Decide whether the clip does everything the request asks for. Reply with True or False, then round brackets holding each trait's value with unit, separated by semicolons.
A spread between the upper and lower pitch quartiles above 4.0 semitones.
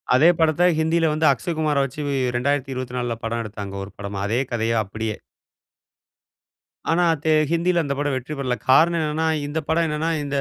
True (4.9 semitones)